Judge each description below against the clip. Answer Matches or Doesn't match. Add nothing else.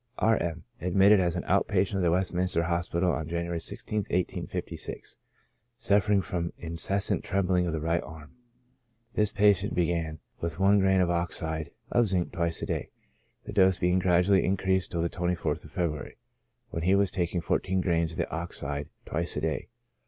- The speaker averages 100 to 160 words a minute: Doesn't match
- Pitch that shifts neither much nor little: Doesn't match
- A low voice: Matches